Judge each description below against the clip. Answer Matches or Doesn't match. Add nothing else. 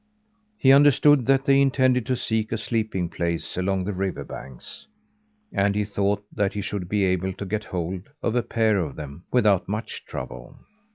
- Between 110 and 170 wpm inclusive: Doesn't match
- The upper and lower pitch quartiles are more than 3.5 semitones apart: Matches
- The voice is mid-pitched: Doesn't match